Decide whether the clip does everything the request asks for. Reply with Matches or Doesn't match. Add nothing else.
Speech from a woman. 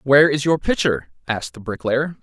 Doesn't match